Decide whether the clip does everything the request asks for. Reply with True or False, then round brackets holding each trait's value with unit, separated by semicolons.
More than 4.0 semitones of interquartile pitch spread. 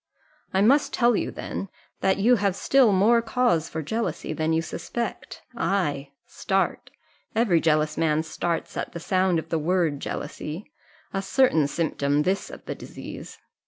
True (5.0 semitones)